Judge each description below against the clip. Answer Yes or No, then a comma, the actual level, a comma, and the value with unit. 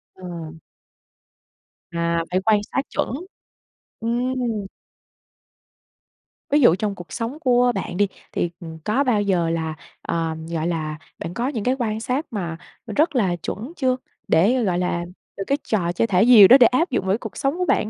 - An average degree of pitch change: No, wide, 6.4 semitones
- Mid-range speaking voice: No, high, 210 Hz